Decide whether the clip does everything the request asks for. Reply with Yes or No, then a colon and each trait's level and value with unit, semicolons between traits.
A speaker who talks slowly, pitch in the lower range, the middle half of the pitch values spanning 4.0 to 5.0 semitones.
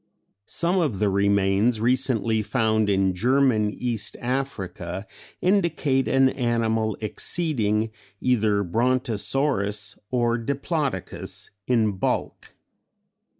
Yes: slow, 90 wpm; low, 115 Hz; average, 4.3 semitones